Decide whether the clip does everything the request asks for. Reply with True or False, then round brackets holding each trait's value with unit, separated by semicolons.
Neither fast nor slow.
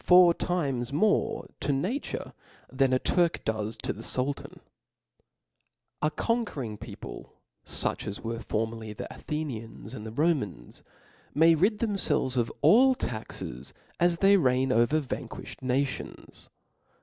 False (130 wpm)